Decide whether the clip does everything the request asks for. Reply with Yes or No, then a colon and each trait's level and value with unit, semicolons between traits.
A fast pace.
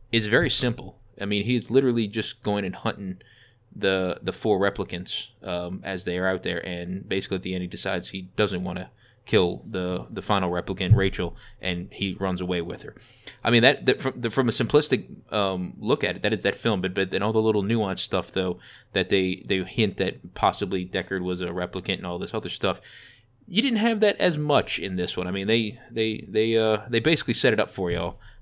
Yes: fast, 225 wpm